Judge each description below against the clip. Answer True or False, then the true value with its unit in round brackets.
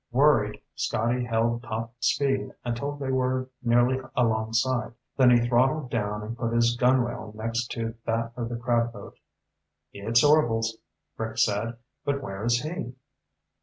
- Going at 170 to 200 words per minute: False (145 wpm)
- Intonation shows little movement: True (2.1 semitones)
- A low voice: True (120 Hz)